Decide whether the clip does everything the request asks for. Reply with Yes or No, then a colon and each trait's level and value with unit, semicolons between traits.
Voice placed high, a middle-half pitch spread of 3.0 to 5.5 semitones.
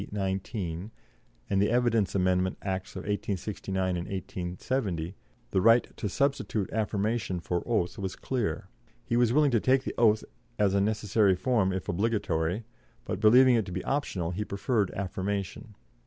No: low, 100 Hz; average, 3.6 semitones